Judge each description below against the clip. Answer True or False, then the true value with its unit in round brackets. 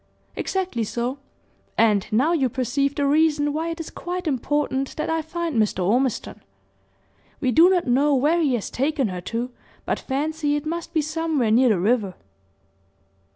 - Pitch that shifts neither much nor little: True (4.7 semitones)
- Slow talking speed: False (165 wpm)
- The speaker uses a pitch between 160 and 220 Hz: False (280 Hz)